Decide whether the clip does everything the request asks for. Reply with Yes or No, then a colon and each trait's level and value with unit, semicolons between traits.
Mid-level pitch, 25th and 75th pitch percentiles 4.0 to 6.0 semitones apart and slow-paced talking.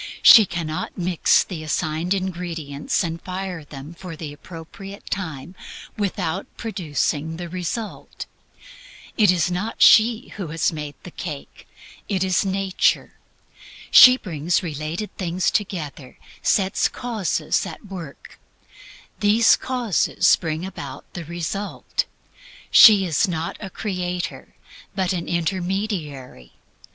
No: medium, 180 Hz; average, 3.5 semitones; slow, 115 wpm